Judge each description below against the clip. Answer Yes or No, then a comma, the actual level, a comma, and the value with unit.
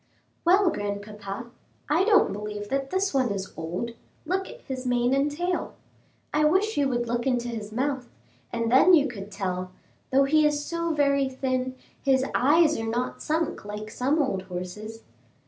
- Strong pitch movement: Yes, wide, 5.9 semitones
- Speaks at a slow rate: No, average, 170 wpm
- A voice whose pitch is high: Yes, very high, 260 Hz